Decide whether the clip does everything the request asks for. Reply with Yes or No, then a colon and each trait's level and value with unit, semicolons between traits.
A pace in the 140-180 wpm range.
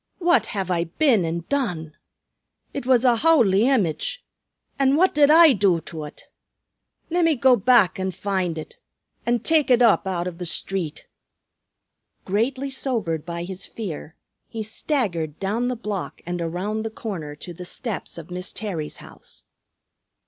Yes: average, 155 wpm